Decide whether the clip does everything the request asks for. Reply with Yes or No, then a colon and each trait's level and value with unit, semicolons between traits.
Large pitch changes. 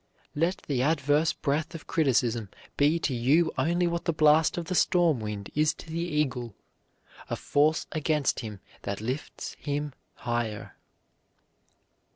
No: average, 4.8 semitones